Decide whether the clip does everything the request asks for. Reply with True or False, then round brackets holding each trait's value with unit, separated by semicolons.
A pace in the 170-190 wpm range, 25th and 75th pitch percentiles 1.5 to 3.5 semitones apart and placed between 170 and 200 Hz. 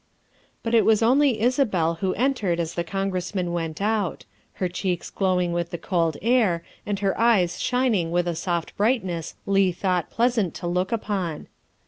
False (180 wpm; 4.3 semitones; 190 Hz)